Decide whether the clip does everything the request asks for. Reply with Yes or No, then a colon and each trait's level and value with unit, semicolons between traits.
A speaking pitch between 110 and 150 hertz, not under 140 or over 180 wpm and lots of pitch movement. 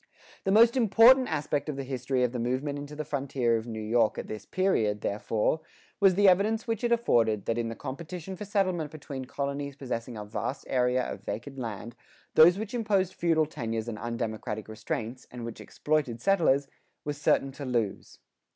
No: low, 135 Hz; average, 190 wpm; wide, 6.9 semitones